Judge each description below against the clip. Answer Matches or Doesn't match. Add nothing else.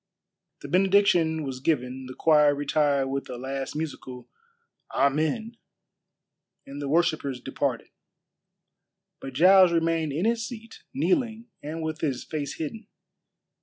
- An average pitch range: Matches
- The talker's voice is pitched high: Doesn't match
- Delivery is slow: Matches